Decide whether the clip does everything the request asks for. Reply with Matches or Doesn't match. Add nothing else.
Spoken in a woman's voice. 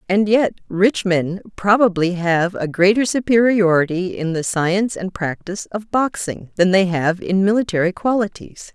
Matches